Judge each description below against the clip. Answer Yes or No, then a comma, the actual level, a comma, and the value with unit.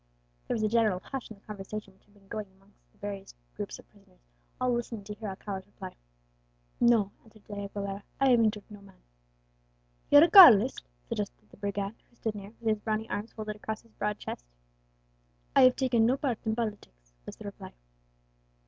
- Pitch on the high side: Yes, high, 210 Hz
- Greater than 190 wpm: Yes, average, 200 wpm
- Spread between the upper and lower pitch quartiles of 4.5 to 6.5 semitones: No, narrow, 2.5 semitones